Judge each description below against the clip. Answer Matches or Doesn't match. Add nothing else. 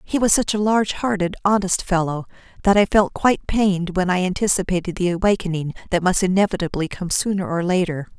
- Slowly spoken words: Doesn't match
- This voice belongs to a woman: Matches